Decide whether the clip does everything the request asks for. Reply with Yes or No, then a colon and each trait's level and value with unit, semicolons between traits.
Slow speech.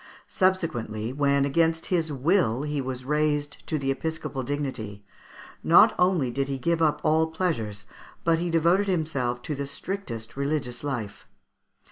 No: average, 145 wpm